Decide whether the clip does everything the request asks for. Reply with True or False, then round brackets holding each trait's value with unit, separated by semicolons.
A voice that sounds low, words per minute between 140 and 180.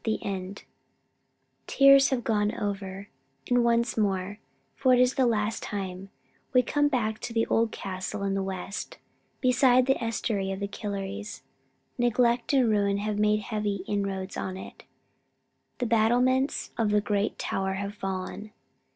False (210 Hz; 150 wpm)